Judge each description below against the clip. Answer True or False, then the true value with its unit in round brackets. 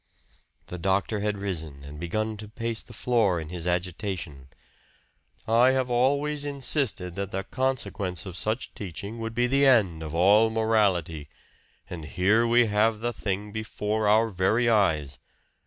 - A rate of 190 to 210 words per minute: False (155 wpm)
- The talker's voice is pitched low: True (105 Hz)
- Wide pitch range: False (4.3 semitones)